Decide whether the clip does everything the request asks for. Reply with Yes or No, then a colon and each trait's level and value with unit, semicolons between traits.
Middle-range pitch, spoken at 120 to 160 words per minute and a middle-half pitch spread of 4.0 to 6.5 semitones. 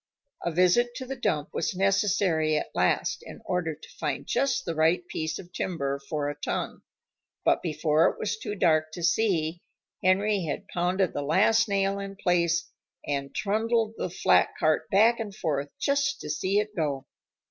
No: medium, 180 Hz; average, 175 wpm; average, 4.7 semitones